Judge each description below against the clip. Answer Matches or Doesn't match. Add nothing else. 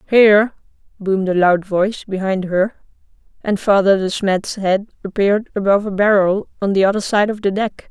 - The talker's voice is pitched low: Doesn't match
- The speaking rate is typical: Matches